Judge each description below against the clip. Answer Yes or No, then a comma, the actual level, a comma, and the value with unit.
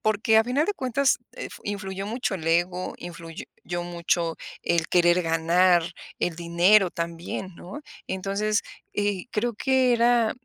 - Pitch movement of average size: Yes, average, 4.2 semitones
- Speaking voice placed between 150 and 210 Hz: Yes, high, 190 Hz